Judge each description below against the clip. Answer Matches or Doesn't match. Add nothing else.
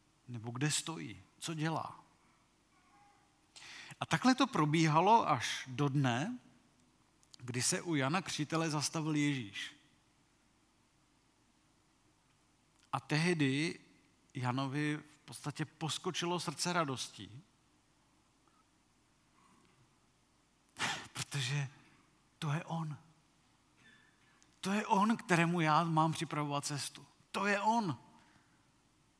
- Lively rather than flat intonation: Doesn't match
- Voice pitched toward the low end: Doesn't match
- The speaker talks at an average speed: Doesn't match